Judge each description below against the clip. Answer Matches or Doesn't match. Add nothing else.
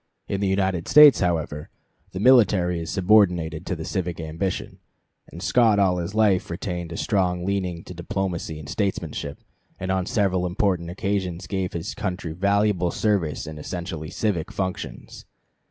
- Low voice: Matches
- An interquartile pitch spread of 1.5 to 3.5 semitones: Matches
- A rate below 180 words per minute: Matches